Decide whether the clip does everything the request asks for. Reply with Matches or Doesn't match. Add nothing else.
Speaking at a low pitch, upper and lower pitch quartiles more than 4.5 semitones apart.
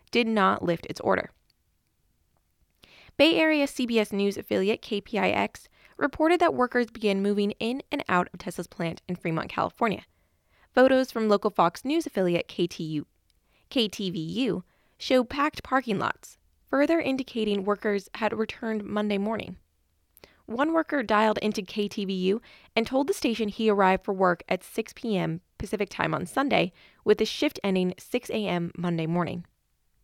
Doesn't match